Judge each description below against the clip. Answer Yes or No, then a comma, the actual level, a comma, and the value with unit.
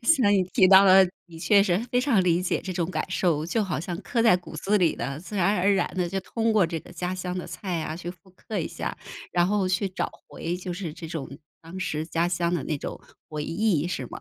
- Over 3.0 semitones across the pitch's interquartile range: No, average, 2.7 semitones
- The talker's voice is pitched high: No, medium, 180 Hz